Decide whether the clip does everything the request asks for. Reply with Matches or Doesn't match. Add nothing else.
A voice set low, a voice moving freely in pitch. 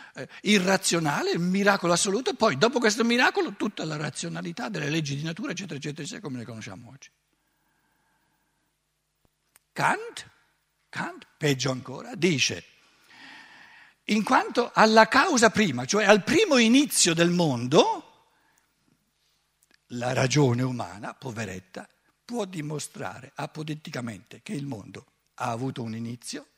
Doesn't match